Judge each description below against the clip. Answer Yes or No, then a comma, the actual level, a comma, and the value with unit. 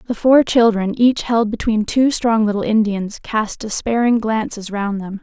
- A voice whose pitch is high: Yes, high, 220 Hz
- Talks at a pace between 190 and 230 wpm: No, average, 170 wpm